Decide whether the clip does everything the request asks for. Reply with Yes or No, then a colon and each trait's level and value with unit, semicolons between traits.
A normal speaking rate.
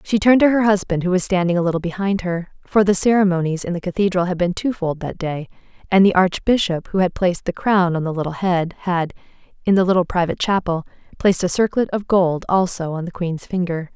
No: fast, 220 wpm